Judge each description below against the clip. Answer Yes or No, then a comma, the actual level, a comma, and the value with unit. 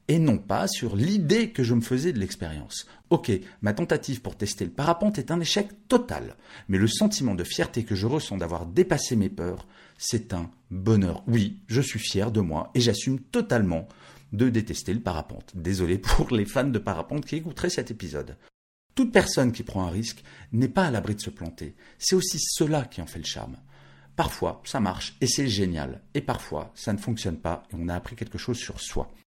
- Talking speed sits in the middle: Yes, average, 205 wpm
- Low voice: Yes, low, 115 Hz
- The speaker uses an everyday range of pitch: No, wide, 6.6 semitones